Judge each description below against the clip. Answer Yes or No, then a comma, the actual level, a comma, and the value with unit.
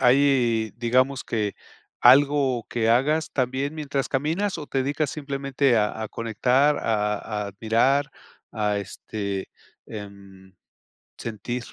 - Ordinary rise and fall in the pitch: Yes, average, 4.5 semitones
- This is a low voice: Yes, low, 125 Hz